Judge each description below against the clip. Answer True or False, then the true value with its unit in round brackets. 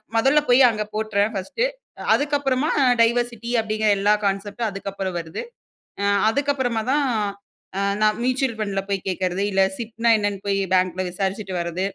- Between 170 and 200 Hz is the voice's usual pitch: False (215 Hz)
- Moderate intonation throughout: True (3.8 semitones)